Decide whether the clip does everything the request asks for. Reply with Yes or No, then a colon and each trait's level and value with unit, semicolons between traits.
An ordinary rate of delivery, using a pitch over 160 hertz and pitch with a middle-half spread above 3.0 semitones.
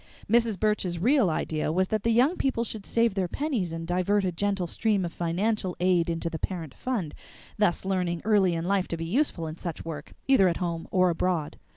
No: fast, 210 wpm; medium, 185 Hz; average, 4.1 semitones